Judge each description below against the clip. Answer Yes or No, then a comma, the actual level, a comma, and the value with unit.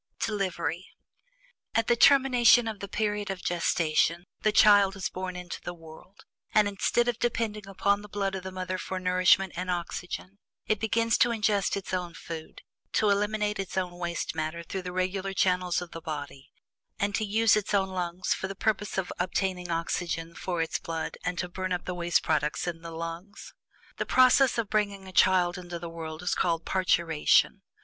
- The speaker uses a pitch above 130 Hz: Yes, medium, 185 Hz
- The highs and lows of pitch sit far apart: No, average, 2.9 semitones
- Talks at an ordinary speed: Yes, average, 190 wpm